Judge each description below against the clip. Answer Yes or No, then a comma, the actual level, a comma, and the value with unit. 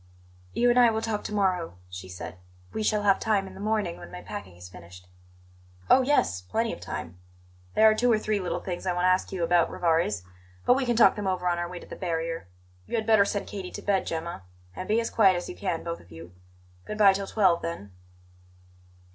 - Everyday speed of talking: No, fast, 235 wpm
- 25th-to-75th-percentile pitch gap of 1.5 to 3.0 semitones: No, average, 4.3 semitones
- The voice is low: No, medium, 185 Hz